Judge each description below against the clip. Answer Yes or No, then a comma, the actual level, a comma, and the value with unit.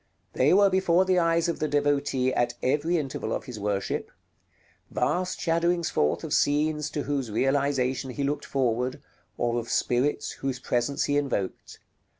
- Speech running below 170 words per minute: Yes, average, 155 wpm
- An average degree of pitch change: Yes, average, 4.2 semitones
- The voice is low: No, medium, 145 Hz